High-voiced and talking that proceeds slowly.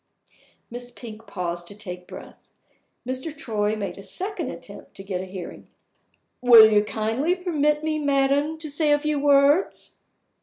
No: very high, 255 Hz; average, 155 wpm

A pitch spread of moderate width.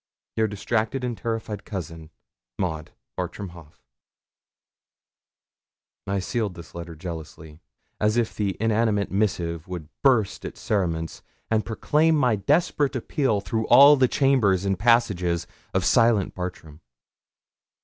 Yes: average, 5.0 semitones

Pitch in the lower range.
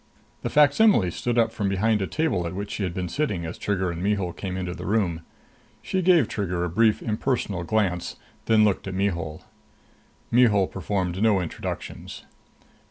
Yes: low, 100 Hz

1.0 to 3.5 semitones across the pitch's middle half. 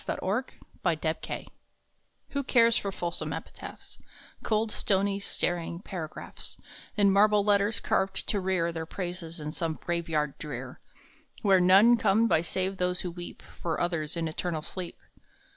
Yes: average, 3.2 semitones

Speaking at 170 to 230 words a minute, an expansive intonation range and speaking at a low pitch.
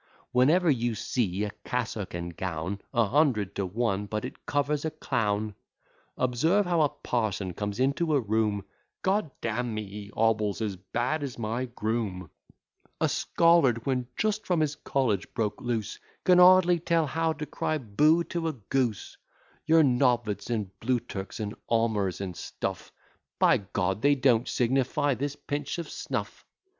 No: average, 160 wpm; wide, 5.9 semitones; low, 120 Hz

